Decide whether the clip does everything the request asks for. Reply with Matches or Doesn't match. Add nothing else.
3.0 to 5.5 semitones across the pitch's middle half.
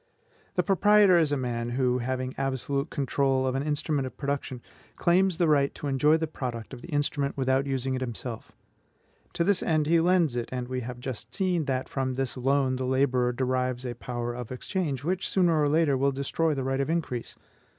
Matches